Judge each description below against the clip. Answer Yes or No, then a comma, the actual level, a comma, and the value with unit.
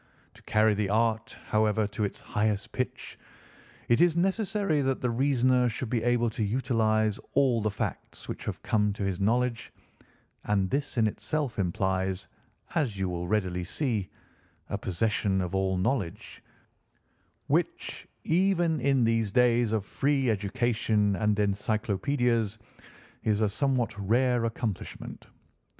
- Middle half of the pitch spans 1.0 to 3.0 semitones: No, average, 3.6 semitones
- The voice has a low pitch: Yes, low, 110 Hz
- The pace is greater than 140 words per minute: No, slow, 135 wpm